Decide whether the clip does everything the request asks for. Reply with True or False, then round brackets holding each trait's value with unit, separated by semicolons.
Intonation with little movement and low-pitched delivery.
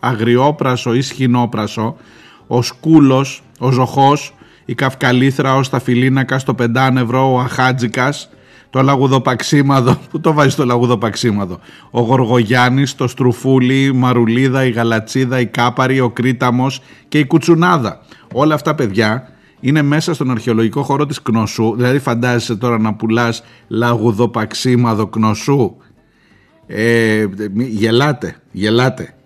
True (2.3 semitones; 125 Hz)